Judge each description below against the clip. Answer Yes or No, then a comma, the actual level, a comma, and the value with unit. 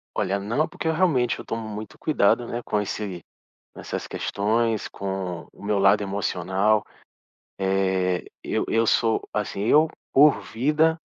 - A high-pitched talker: No, low, 105 Hz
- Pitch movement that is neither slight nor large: Yes, average, 3.8 semitones